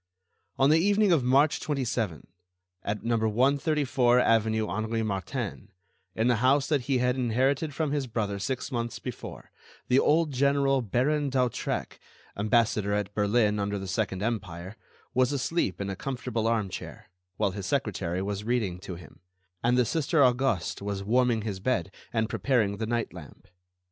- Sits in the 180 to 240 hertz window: No, low, 115 Hz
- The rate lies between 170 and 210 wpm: No, average, 160 wpm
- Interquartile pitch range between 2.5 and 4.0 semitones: No, average, 4.6 semitones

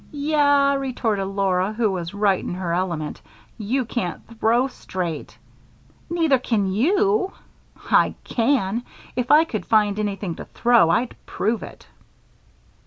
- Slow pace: Yes, slow, 130 wpm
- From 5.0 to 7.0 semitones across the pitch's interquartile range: Yes, wide, 5.4 semitones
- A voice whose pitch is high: Yes, high, 220 Hz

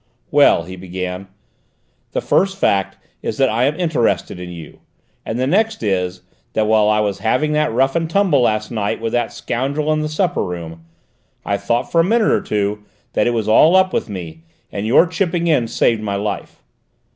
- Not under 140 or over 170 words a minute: No, average, 190 wpm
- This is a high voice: No, low, 115 Hz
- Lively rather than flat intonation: Yes, wide, 7.3 semitones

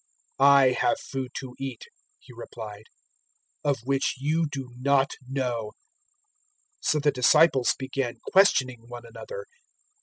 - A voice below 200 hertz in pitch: Yes, low, 135 Hz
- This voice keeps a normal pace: No, slow, 130 wpm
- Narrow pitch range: Yes, narrow, 2.3 semitones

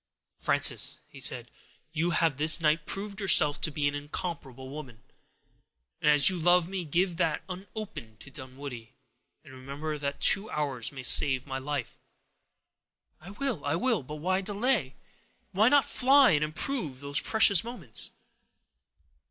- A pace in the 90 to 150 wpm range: Yes, average, 145 wpm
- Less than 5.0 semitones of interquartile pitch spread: No, average, 5.3 semitones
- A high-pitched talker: No, medium, 155 Hz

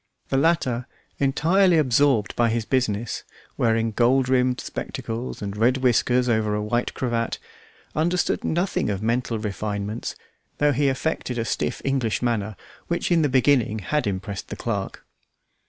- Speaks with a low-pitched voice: Yes, low, 120 Hz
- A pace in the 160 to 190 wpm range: No, average, 145 wpm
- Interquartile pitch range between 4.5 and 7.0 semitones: No, average, 3.7 semitones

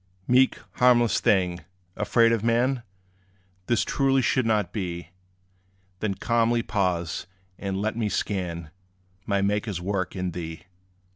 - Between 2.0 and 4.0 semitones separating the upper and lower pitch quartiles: No, average, 4.4 semitones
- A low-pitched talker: Yes, low, 105 Hz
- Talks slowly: Yes, slow, 125 wpm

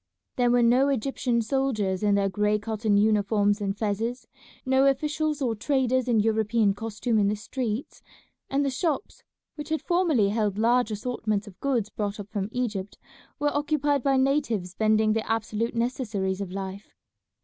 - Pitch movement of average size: Yes, average, 4.2 semitones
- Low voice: No, high, 225 Hz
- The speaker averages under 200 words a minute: Yes, average, 160 wpm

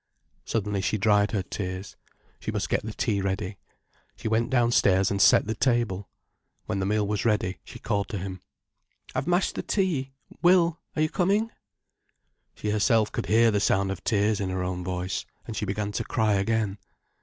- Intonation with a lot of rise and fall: No, average, 3.0 semitones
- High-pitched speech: No, low, 105 Hz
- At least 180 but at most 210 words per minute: Yes, average, 185 wpm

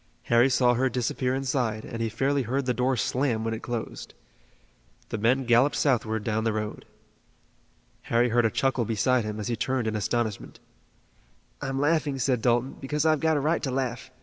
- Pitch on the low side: Yes, low, 125 Hz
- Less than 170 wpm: No, average, 185 wpm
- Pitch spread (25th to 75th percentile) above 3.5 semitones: No, average, 2.9 semitones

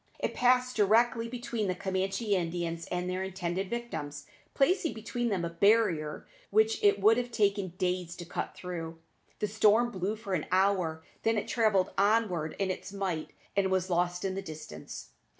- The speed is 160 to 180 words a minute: Yes, average, 170 wpm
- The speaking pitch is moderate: No, high, 195 Hz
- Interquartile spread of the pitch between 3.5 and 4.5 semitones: Yes, average, 4.2 semitones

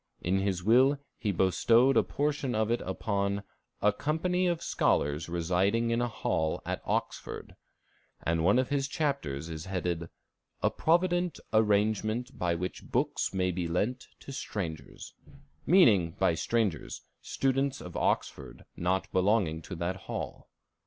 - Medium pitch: No, low, 100 Hz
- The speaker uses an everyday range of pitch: No, wide, 6.4 semitones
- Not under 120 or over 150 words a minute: Yes, average, 140 wpm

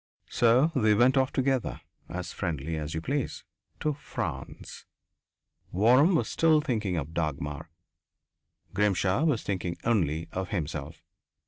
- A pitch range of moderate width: No, wide, 8.1 semitones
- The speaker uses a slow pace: Yes, slow, 125 wpm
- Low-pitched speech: Yes, low, 100 Hz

